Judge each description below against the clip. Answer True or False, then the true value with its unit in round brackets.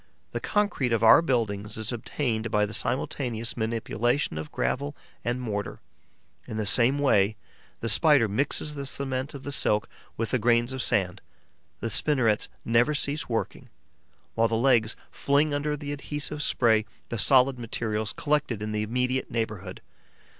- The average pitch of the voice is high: False (120 Hz)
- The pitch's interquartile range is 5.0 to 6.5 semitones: False (4.2 semitones)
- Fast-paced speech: False (155 wpm)